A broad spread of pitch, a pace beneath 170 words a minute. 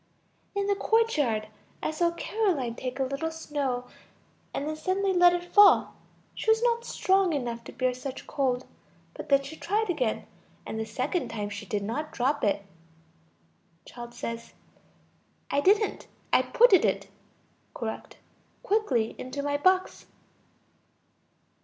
Yes: wide, 7.2 semitones; average, 140 wpm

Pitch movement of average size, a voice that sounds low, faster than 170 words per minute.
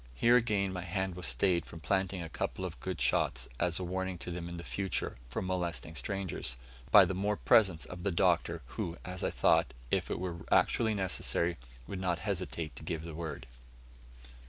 No: narrow, 2.2 semitones; very low, 90 Hz; average, 190 wpm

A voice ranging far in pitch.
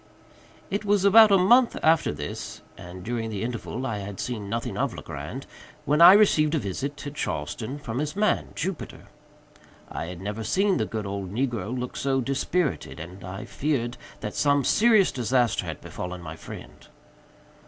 Yes: wide, 7.8 semitones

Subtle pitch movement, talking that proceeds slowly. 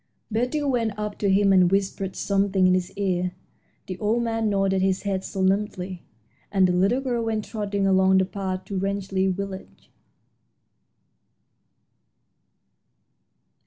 Yes: narrow, 1.8 semitones; slow, 130 wpm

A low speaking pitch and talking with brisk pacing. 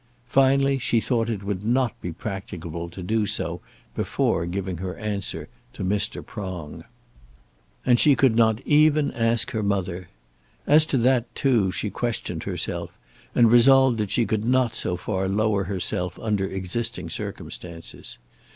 No: low, 110 Hz; average, 150 wpm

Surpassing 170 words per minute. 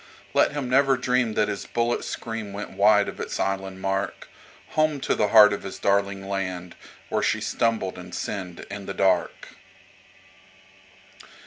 No: average, 150 wpm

